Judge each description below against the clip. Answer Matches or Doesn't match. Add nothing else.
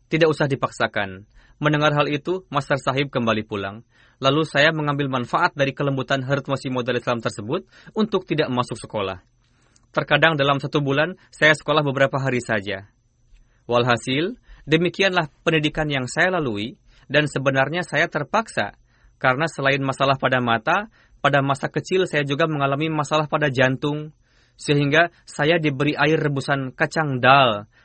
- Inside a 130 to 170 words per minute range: Matches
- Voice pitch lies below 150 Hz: Matches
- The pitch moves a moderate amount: Matches